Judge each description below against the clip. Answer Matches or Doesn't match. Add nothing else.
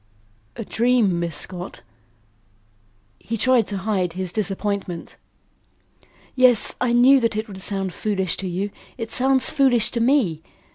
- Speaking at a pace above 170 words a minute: Doesn't match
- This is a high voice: Matches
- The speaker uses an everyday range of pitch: Matches